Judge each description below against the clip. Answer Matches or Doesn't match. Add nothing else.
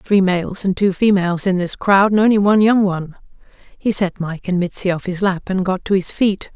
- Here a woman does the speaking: Matches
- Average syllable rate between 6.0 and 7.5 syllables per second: Doesn't match